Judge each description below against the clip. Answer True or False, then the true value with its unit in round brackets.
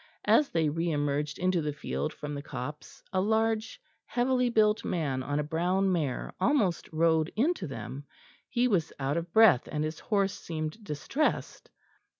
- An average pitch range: False (6.2 semitones)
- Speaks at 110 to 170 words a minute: True (160 wpm)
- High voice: False (165 Hz)